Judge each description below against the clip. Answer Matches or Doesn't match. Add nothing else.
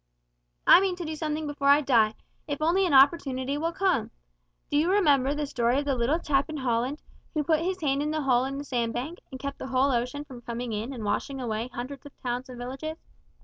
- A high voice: Matches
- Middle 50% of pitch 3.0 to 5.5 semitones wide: Matches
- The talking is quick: Matches